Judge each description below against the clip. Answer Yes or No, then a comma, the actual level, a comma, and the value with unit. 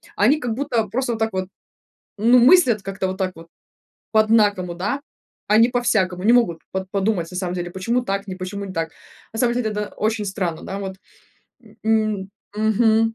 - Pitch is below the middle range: No, high, 205 Hz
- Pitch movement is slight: No, average, 3.3 semitones